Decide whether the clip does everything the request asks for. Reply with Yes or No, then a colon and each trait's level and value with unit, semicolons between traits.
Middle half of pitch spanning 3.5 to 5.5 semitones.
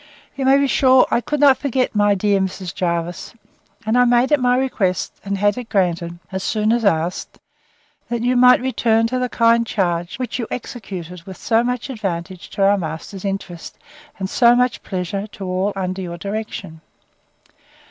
Yes: average, 5.0 semitones